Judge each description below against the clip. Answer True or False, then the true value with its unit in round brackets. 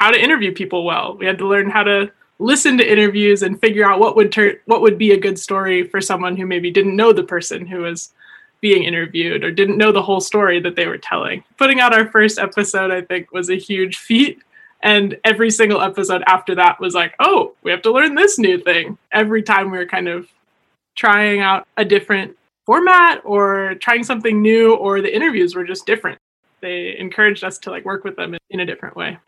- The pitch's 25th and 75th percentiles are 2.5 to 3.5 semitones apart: True (3.0 semitones)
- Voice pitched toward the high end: True (200 Hz)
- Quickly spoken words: True (220 wpm)